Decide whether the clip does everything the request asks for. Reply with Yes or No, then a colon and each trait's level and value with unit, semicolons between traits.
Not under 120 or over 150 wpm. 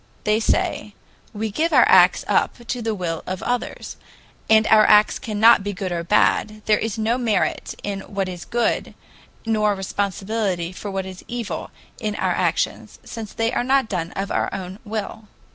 No: average, 180 wpm